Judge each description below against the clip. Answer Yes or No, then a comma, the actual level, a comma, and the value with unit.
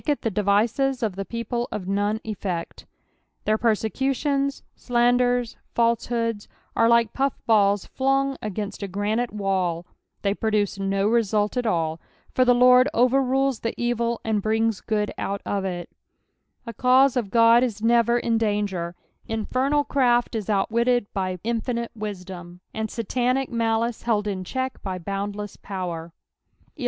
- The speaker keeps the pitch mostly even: No, average, 3.3 semitones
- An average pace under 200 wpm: Yes, average, 145 wpm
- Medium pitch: No, high, 225 Hz